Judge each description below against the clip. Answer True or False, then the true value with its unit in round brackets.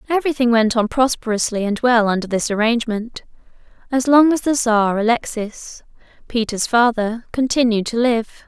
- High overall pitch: True (235 Hz)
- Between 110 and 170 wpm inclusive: True (150 wpm)